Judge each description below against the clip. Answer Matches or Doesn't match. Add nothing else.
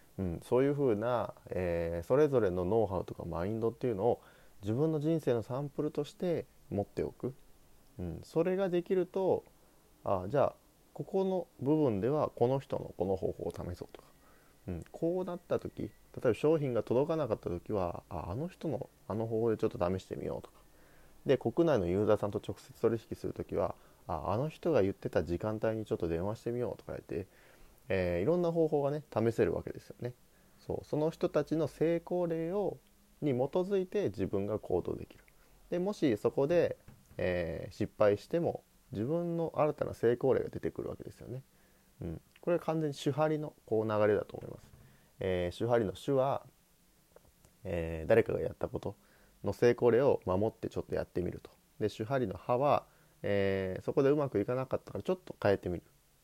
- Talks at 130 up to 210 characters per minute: Doesn't match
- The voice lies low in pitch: Matches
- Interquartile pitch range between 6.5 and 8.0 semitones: Matches